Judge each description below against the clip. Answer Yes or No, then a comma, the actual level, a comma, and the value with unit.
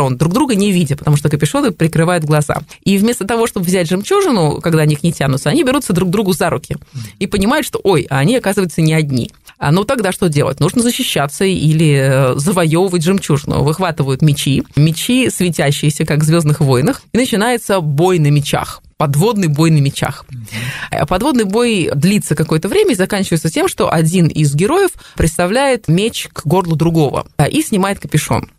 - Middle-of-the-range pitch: Yes, medium, 170 Hz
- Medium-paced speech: No, fast, 170 wpm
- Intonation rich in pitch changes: No, average, 4.9 semitones